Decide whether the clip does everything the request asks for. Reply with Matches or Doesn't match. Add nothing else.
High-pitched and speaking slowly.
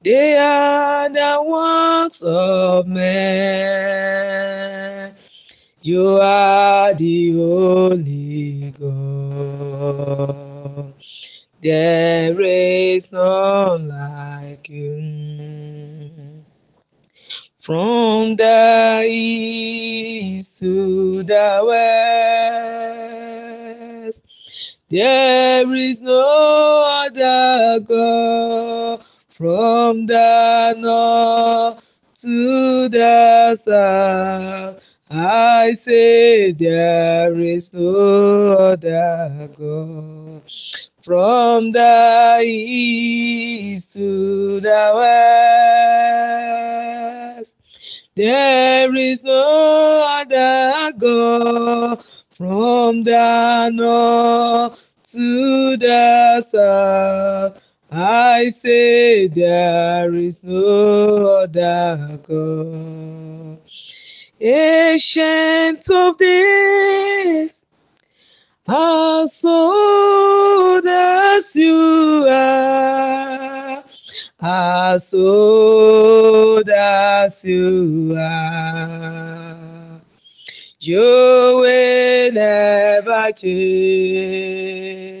Matches